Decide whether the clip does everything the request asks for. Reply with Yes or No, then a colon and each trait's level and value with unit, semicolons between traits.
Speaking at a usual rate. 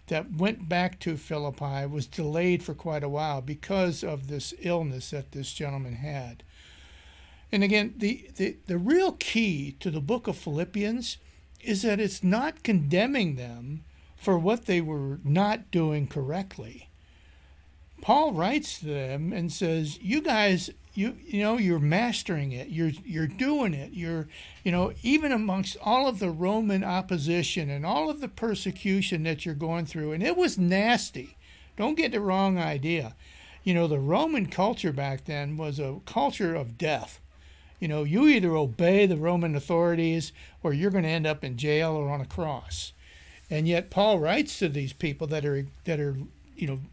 Yes: average, 175 wpm